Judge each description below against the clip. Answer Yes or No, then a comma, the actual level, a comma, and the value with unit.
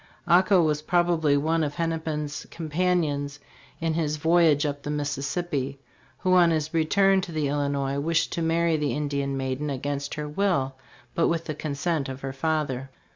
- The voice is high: No, medium, 150 Hz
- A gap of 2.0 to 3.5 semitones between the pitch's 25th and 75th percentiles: Yes, average, 2.8 semitones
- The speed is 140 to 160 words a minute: No, average, 170 wpm